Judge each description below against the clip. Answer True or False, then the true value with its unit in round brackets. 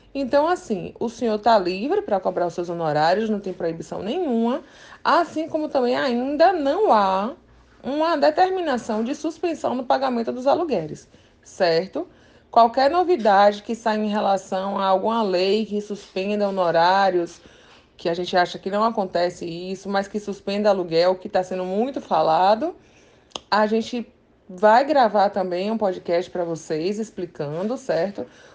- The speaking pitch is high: True (210 Hz)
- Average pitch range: False (5.8 semitones)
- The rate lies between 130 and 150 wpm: True (145 wpm)